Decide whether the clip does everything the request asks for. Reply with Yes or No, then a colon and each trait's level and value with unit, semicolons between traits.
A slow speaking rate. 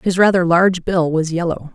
No: fast, 205 wpm